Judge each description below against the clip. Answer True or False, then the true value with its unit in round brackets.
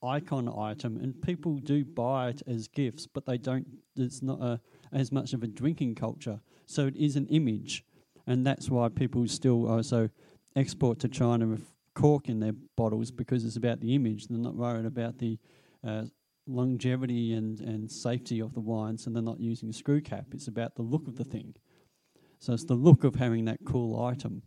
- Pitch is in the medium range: False (120 Hz)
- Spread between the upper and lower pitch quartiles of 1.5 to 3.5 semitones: True (2.9 semitones)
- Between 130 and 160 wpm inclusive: False (200 wpm)